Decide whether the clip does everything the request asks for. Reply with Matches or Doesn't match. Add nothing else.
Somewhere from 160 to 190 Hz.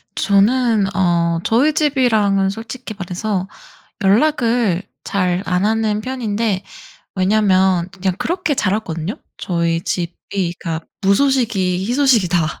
Doesn't match